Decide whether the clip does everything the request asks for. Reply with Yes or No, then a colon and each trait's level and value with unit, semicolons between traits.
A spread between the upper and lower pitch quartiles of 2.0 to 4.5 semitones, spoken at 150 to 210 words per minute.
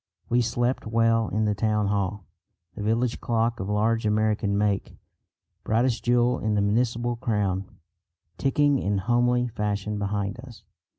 No: narrow, 2.6 semitones; average, 140 wpm